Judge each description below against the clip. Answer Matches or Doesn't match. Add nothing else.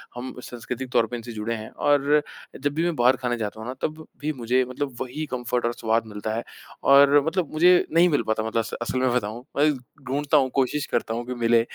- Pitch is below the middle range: Matches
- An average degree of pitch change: Matches